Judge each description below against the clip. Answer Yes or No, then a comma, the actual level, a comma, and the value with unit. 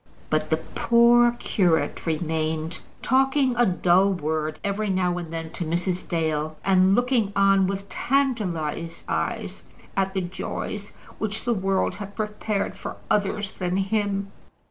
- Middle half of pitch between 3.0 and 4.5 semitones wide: Yes, average, 3.9 semitones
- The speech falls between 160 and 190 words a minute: No, average, 140 wpm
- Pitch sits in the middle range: No, high, 195 Hz